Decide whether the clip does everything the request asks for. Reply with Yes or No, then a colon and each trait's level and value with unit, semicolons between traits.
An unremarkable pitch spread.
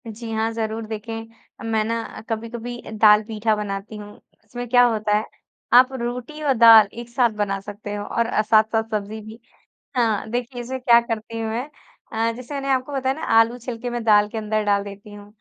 No: narrow, 2.2 semitones